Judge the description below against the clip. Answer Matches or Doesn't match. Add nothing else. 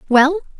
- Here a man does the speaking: Doesn't match